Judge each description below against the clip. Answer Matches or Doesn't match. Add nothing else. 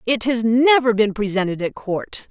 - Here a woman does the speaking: Matches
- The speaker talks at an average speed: Matches